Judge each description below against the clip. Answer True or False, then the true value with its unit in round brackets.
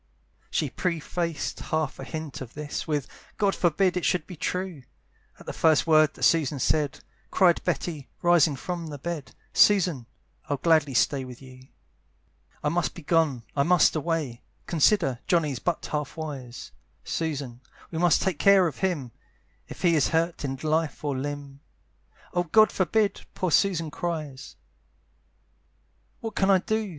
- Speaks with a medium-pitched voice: True (155 Hz)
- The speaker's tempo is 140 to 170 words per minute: True (155 wpm)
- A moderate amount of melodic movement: True (3.7 semitones)